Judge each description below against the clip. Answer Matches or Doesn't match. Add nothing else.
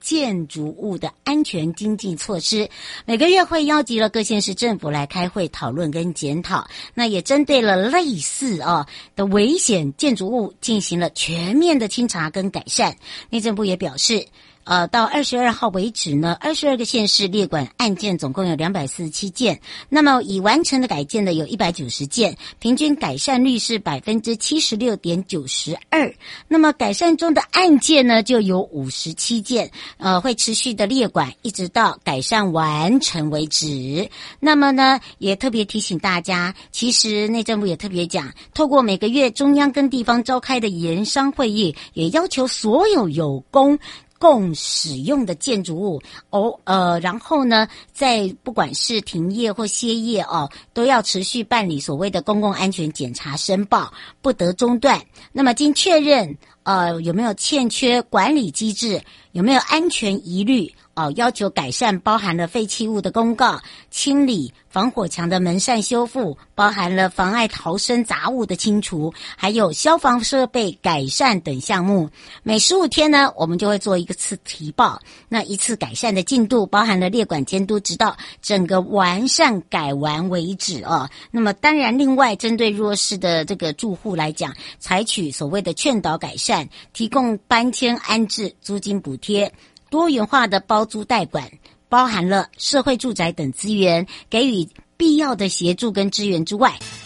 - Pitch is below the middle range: Doesn't match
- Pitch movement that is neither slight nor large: Doesn't match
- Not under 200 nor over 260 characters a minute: Matches